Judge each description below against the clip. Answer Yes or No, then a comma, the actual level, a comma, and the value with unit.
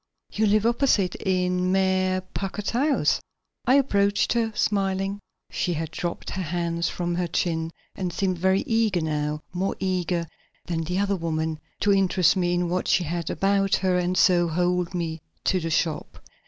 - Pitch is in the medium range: Yes, medium, 180 Hz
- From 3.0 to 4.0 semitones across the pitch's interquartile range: No, narrow, 2.4 semitones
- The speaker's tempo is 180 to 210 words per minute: No, average, 170 wpm